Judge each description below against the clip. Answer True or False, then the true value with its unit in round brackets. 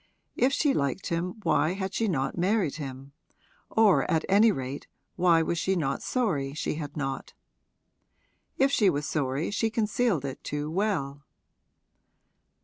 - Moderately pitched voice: True (165 Hz)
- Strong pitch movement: True (6.4 semitones)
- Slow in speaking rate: False (145 wpm)